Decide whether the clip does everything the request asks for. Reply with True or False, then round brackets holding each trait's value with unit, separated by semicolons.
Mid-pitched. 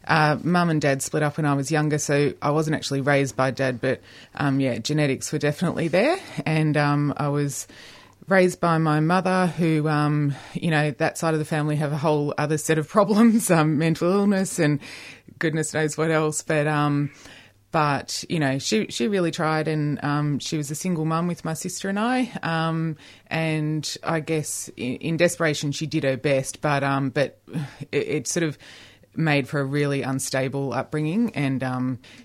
True (150 Hz)